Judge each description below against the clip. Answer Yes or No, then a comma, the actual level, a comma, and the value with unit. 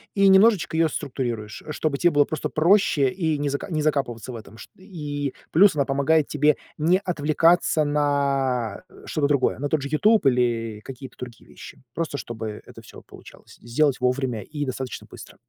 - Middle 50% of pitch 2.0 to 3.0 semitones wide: No, average, 3.8 semitones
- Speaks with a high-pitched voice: No, medium, 145 Hz